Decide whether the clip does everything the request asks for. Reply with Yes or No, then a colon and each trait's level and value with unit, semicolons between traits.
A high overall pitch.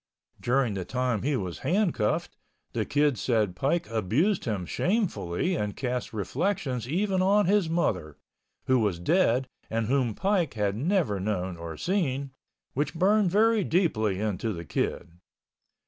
No: low, 130 Hz